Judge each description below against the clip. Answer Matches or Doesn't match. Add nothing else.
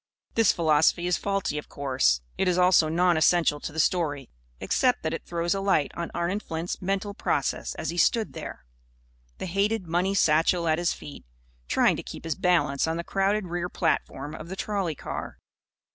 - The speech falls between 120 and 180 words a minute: Doesn't match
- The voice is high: Doesn't match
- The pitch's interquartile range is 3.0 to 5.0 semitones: Matches